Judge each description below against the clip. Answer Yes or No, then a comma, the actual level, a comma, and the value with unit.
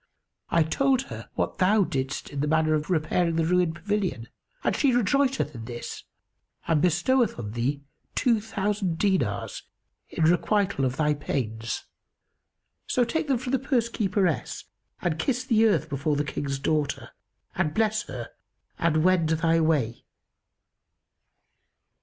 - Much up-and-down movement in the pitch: Yes, wide, 6.4 semitones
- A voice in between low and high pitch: Yes, medium, 170 Hz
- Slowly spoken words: No, average, 145 wpm